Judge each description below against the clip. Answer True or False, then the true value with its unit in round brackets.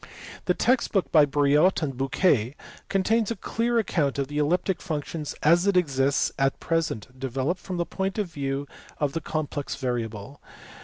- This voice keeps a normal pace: True (160 wpm)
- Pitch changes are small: False (5.1 semitones)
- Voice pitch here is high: False (150 Hz)